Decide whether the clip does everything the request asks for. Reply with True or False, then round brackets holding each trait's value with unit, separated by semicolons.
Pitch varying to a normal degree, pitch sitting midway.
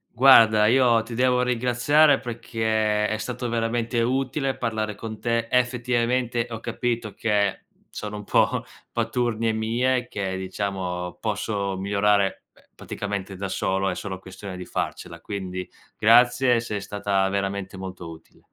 False (3.4 semitones; 110 Hz)